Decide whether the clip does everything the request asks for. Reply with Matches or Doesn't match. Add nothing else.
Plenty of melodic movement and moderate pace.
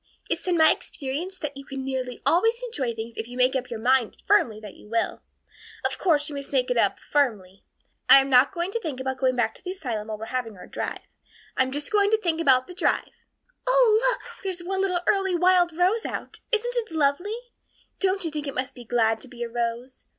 Doesn't match